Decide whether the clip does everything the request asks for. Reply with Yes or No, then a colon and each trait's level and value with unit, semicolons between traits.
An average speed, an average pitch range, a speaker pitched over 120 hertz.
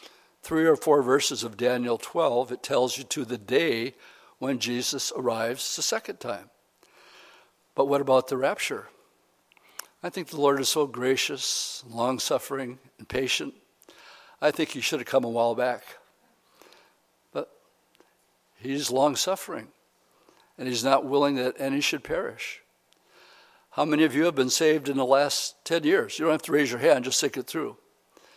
Yes: average, 165 wpm; average, 3.7 semitones; medium, 140 Hz